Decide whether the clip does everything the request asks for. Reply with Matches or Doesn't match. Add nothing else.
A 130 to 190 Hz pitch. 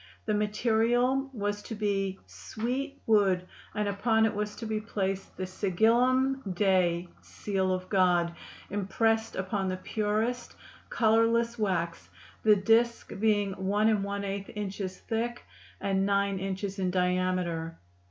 Doesn't match